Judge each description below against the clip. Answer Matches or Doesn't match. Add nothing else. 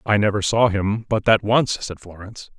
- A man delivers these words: Matches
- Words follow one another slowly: Doesn't match